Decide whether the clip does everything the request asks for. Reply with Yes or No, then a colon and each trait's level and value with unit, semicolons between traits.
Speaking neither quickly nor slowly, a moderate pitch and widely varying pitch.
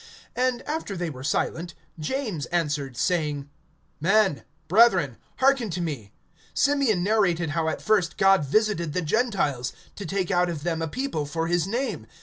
Yes: average, 155 wpm; medium, 175 Hz; wide, 5.9 semitones